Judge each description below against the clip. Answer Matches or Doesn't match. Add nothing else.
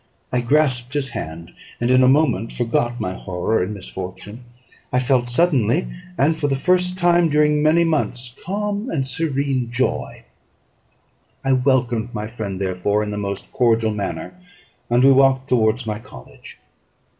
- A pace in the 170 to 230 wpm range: Doesn't match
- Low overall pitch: Matches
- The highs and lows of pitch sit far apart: Doesn't match